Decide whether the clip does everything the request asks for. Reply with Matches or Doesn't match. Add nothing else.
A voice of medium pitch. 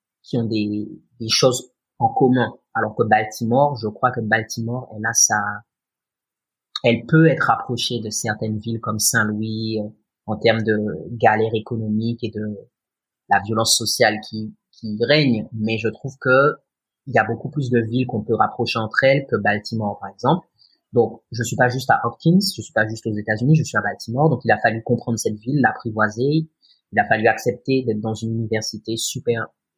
Doesn't match